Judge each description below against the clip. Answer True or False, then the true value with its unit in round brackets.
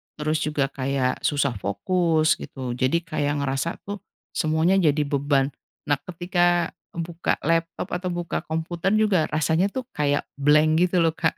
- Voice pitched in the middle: True (160 Hz)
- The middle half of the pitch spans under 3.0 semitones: False (3.3 semitones)